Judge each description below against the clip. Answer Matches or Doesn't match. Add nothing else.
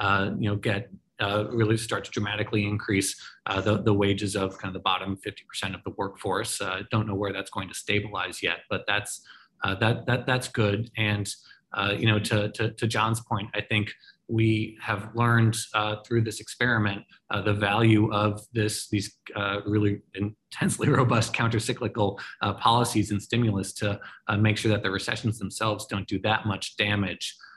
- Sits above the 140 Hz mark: Doesn't match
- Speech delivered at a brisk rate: Doesn't match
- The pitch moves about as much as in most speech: Doesn't match